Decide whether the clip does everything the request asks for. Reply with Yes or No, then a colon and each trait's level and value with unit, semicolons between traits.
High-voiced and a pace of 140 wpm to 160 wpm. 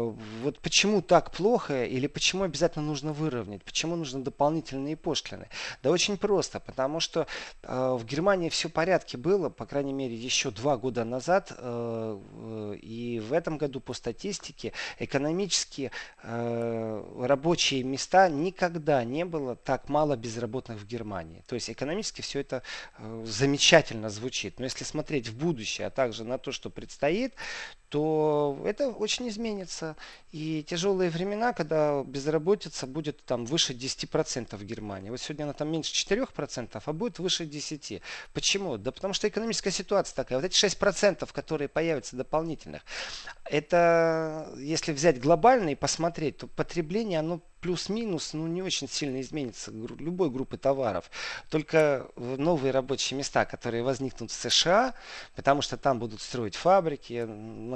No: medium, 145 Hz; average, 145 wpm